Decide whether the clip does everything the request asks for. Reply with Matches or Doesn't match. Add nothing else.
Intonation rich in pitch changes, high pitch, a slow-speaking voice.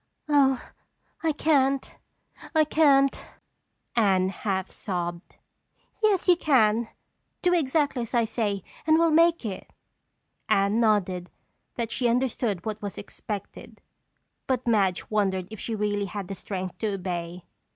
Matches